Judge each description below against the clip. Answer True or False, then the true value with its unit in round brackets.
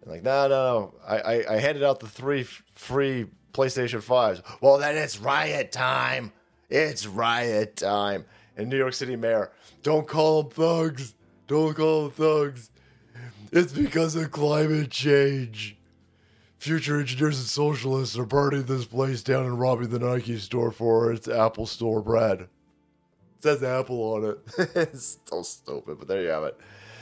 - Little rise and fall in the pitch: False (4.5 semitones)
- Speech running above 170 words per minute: False (160 wpm)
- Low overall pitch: True (130 Hz)